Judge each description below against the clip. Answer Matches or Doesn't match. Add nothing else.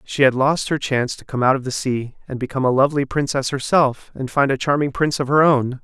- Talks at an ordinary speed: Doesn't match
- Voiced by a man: Matches